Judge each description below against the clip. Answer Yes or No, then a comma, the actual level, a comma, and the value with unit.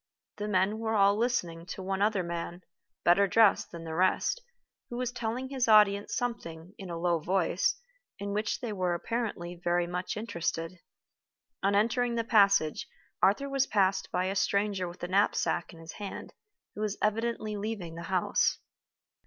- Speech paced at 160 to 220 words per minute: Yes, average, 170 wpm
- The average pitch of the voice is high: Yes, high, 200 Hz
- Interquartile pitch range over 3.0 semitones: Yes, average, 3.9 semitones